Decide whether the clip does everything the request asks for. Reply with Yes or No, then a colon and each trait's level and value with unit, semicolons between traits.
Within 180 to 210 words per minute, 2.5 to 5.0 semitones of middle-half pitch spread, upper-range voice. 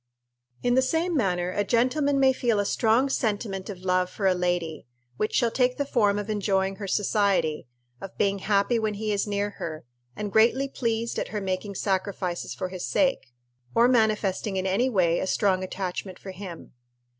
Yes: average, 185 wpm; average, 3.7 semitones; high, 205 Hz